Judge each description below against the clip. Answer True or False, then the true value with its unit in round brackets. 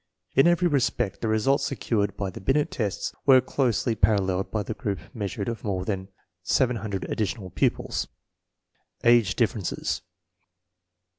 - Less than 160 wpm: True (140 wpm)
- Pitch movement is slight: False (4.0 semitones)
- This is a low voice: True (110 Hz)